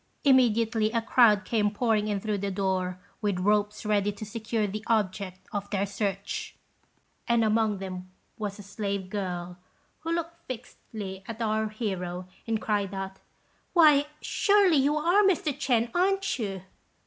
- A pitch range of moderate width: Yes, average, 3.4 semitones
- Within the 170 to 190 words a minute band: No, average, 150 wpm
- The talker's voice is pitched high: Yes, high, 215 Hz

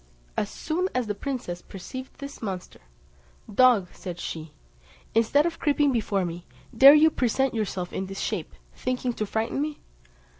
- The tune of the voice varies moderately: No, wide, 6.2 semitones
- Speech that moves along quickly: No, average, 155 wpm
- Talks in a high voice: Yes, high, 230 Hz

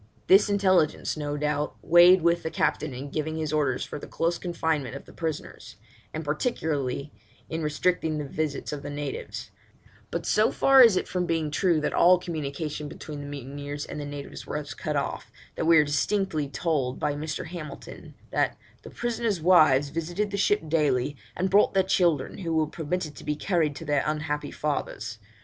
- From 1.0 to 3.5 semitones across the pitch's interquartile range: Yes, average, 3.1 semitones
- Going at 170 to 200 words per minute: Yes, average, 185 wpm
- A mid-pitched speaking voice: Yes, medium, 155 Hz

